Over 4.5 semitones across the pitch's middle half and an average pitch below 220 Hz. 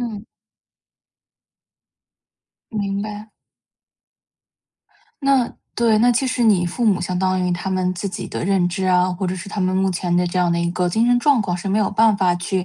No: average, 3.2 semitones; high, 190 Hz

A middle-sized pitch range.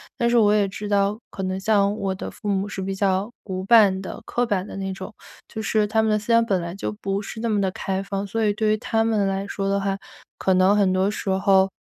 No: narrow, 1.8 semitones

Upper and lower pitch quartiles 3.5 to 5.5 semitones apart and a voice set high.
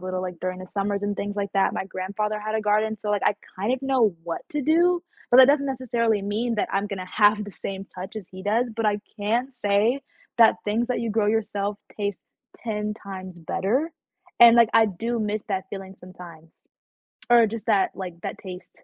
No: average, 2.9 semitones; high, 210 Hz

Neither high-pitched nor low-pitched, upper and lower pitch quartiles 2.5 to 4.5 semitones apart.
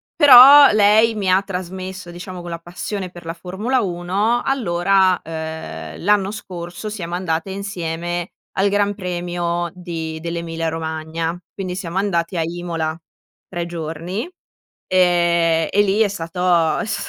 Yes: medium, 175 Hz; average, 2.8 semitones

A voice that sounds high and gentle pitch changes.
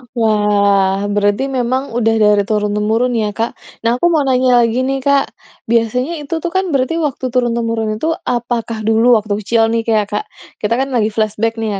No: high, 230 Hz; average, 3.2 semitones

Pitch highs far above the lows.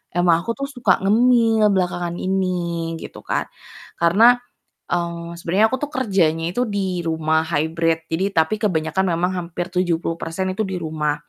No: average, 3.4 semitones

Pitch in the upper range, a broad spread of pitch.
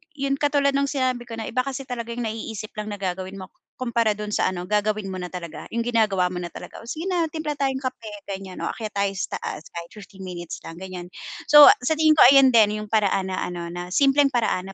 Yes: high, 215 Hz; wide, 5.7 semitones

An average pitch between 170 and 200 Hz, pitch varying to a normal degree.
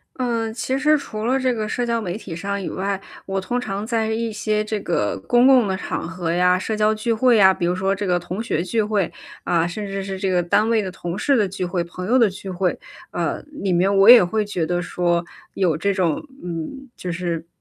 Yes: high, 195 Hz; average, 3.8 semitones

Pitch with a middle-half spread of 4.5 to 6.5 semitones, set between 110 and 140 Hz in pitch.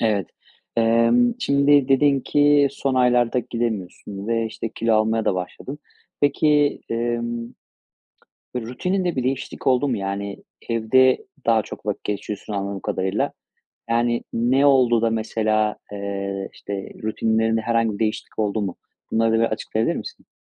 No: average, 3.2 semitones; low, 115 Hz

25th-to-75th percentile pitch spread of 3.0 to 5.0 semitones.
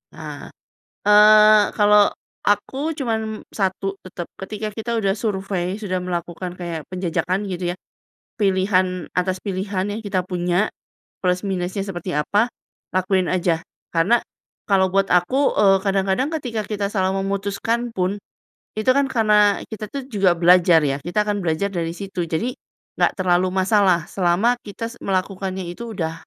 No: narrow, 2.5 semitones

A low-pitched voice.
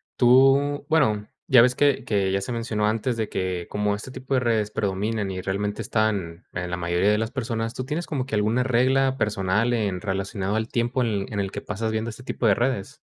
Yes: low, 110 Hz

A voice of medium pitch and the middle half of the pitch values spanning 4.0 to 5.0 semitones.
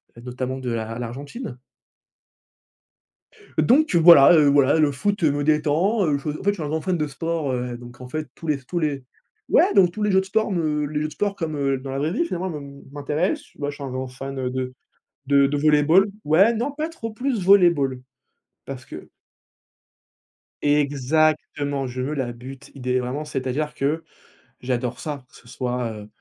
Yes: medium, 145 Hz; average, 4.3 semitones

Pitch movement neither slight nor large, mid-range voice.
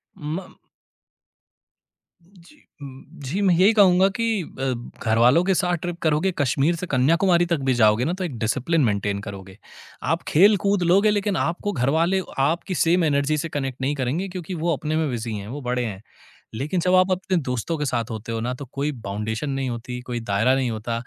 No: wide, 6.5 semitones; medium, 145 Hz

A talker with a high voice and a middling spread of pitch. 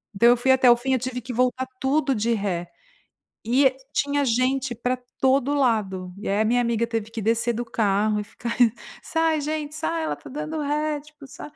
Yes: very high, 250 Hz; average, 3.8 semitones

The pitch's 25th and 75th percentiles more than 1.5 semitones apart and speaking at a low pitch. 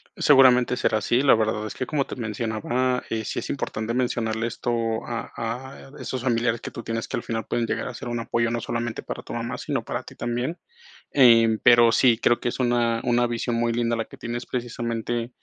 No: narrow, 1.1 semitones; low, 120 Hz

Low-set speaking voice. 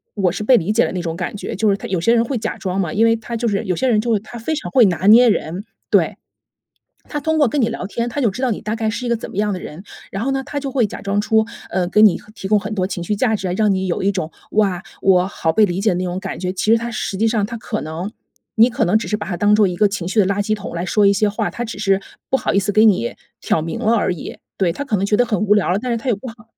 No: high, 210 Hz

